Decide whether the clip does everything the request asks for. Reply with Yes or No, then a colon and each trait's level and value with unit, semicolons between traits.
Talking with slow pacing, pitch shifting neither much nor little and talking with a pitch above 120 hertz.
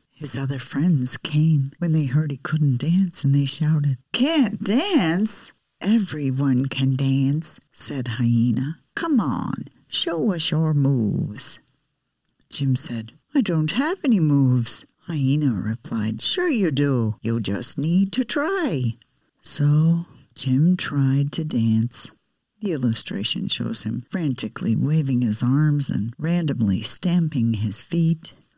Yes: slow, 130 wpm; average, 4.9 semitones; medium, 140 Hz